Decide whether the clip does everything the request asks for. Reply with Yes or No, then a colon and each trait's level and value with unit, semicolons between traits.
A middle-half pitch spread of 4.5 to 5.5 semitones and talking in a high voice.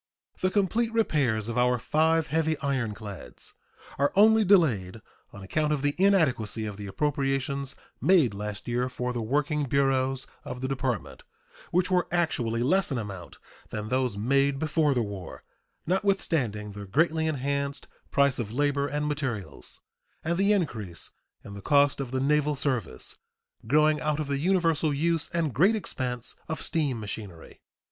No: average, 5.1 semitones; medium, 140 Hz